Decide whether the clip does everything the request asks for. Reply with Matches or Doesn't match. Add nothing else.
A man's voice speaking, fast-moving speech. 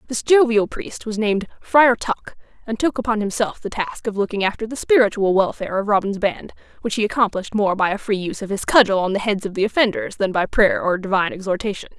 Doesn't match